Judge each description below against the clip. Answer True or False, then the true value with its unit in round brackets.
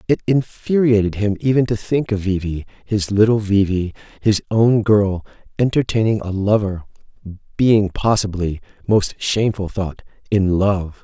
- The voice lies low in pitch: True (105 Hz)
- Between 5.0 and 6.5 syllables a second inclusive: False (4.5 syllables/s)